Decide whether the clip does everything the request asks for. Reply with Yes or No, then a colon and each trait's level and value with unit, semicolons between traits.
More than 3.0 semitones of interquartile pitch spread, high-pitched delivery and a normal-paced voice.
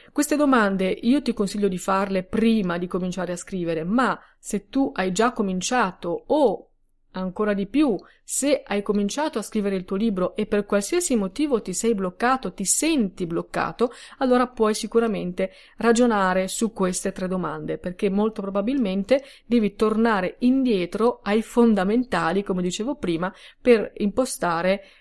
Yes: average, 4.0 semitones; high, 205 Hz; average, 145 wpm